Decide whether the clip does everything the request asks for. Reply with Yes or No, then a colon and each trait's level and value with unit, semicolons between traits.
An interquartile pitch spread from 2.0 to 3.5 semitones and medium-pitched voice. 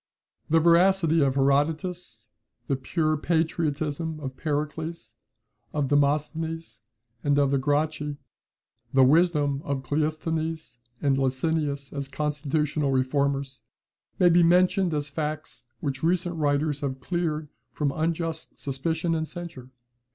Yes: narrow, 2.6 semitones; medium, 150 Hz